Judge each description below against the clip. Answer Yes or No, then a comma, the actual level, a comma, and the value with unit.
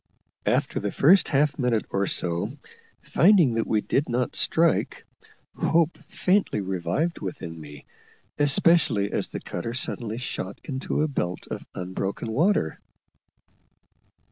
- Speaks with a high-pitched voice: No, low, 120 Hz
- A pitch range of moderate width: No, wide, 8.2 semitones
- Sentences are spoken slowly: Yes, slow, 125 wpm